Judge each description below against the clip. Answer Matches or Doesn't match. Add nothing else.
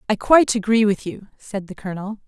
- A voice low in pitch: Doesn't match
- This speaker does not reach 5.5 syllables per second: Doesn't match